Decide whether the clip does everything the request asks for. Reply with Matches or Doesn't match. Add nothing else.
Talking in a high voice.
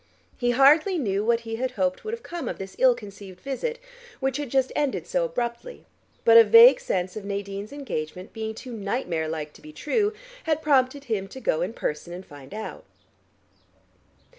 Matches